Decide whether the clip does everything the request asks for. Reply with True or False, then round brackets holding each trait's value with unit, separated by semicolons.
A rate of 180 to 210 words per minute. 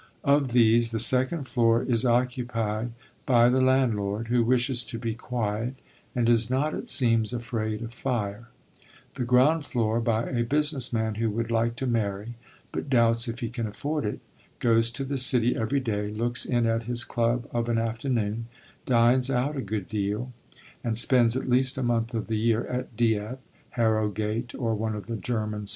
True (185 wpm)